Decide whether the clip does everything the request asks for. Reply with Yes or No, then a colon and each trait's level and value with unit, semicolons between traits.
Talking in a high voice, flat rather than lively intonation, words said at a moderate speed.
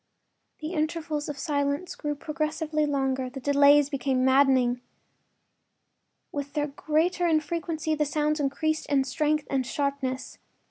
No: very high, 290 Hz; narrow, 2.0 semitones; slow, 125 wpm